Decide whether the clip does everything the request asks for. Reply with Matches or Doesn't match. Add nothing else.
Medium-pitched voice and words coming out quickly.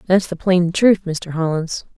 Doesn't match